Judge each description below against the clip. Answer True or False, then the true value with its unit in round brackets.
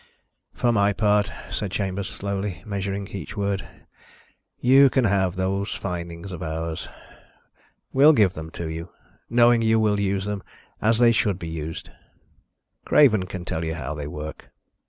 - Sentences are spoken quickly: False (155 wpm)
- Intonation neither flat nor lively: True (3.7 semitones)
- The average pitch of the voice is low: True (100 Hz)